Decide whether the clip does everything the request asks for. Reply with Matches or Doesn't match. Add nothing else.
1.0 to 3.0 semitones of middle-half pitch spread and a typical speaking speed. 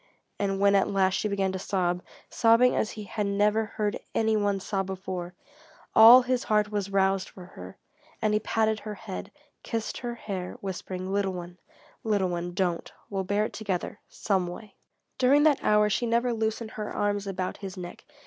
Matches